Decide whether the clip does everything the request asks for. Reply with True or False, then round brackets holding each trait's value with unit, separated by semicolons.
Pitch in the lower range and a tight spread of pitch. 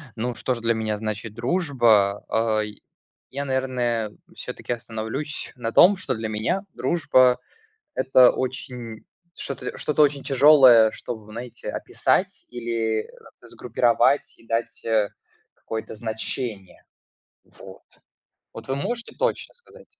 False (120 Hz; 3.2 semitones)